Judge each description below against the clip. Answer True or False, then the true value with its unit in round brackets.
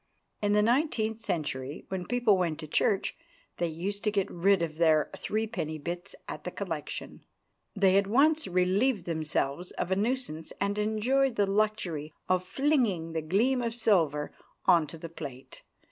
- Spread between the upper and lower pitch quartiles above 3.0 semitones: True (5.1 semitones)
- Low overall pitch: False (190 Hz)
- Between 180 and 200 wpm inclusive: False (160 wpm)